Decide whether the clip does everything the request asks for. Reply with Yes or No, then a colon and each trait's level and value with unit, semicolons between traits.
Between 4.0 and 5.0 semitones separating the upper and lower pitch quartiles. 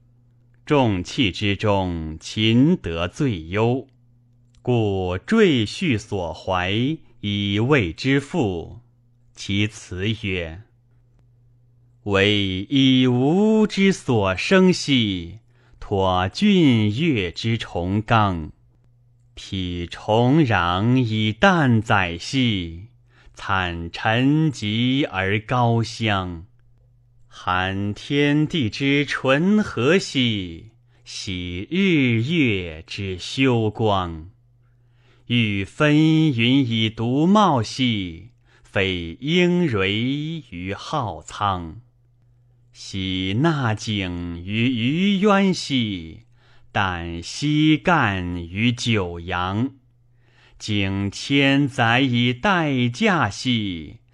Yes: average, 4.5 semitones